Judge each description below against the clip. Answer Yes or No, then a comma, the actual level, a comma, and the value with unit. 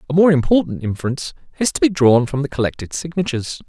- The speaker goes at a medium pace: Yes, average, 195 wpm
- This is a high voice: No, medium, 145 Hz